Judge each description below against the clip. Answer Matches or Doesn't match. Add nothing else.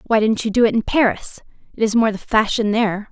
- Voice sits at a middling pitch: Doesn't match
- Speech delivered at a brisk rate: Matches